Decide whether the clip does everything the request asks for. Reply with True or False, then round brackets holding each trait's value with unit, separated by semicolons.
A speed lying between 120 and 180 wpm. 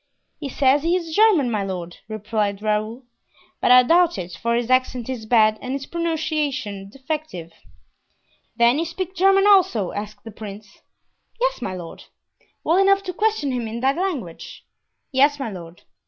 True (165 wpm)